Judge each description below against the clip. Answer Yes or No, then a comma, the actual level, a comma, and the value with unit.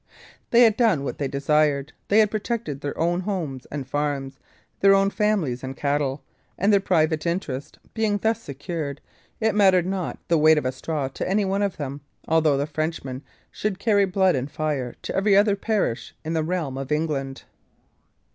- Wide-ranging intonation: Yes, wide, 5.9 semitones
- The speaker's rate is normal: Yes, average, 185 wpm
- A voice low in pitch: No, medium, 160 Hz